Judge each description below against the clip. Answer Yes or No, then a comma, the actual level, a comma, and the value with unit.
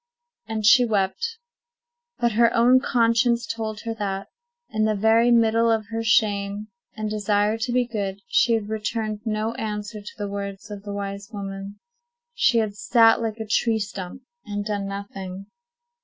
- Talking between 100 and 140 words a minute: No, average, 165 wpm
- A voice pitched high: Yes, high, 215 Hz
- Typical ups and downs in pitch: No, narrow, 2.1 semitones